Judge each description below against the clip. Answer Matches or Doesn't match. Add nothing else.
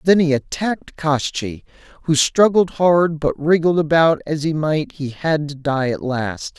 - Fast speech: Doesn't match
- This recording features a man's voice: Matches